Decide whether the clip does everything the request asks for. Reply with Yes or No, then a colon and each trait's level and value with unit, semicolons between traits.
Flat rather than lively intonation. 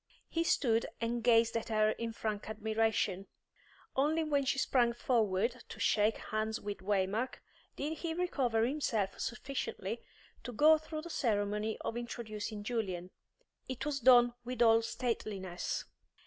No: average, 3.1 semitones